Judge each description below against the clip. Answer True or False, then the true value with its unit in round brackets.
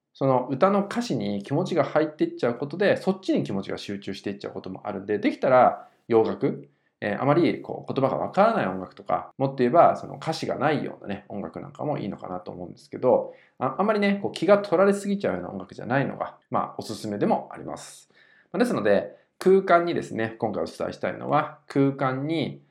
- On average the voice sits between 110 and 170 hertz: True (140 Hz)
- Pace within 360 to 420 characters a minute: False (450 characters per minute)